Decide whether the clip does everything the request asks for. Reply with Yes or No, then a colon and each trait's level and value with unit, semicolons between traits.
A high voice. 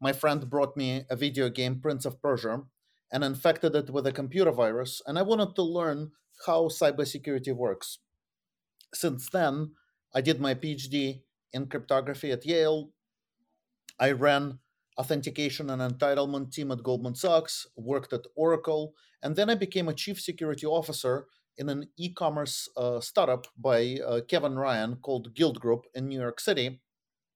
No: medium, 140 Hz